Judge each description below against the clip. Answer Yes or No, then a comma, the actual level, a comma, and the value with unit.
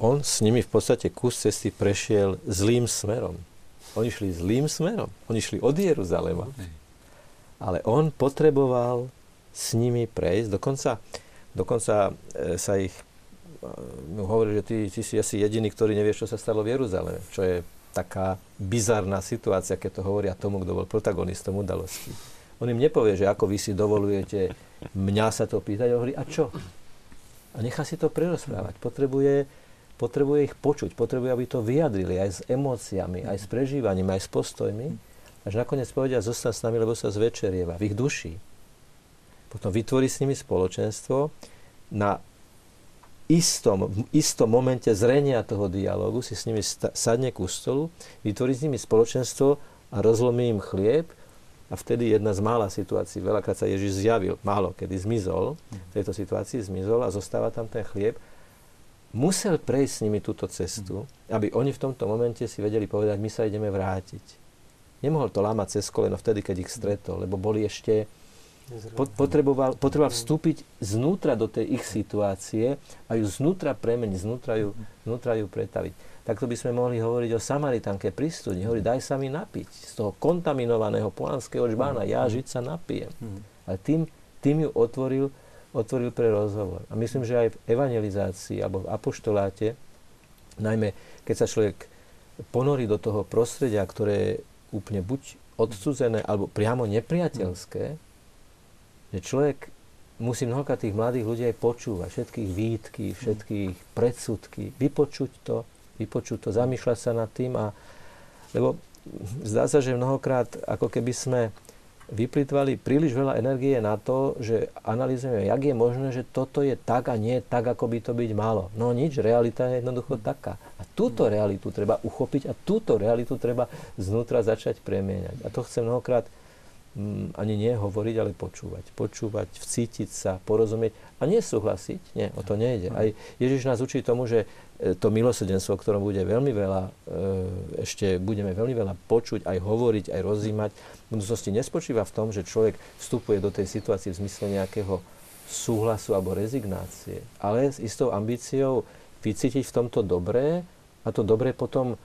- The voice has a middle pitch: No, low, 115 Hz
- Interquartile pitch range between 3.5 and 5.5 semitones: Yes, average, 3.8 semitones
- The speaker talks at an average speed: Yes, average, 155 wpm